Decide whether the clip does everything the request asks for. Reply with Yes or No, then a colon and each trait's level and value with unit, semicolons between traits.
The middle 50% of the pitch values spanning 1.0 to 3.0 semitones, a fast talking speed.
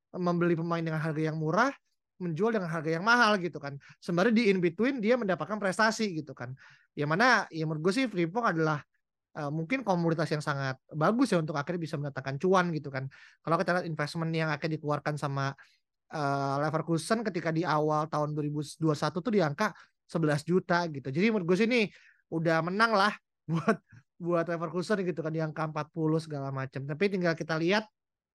No: average, 3.9 semitones; fast, 180 wpm